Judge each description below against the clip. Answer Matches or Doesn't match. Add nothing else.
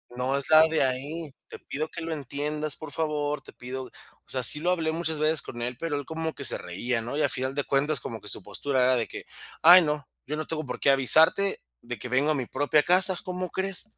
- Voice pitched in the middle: Matches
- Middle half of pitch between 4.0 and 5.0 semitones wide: Doesn't match